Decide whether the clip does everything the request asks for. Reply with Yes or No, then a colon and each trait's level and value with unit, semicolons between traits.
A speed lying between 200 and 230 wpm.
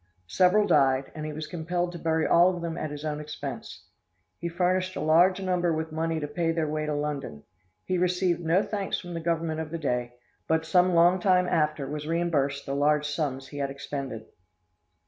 Yes: fast, 205 wpm